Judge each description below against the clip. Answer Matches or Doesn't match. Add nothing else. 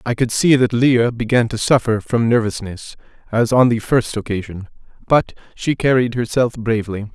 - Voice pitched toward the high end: Doesn't match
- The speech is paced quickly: Doesn't match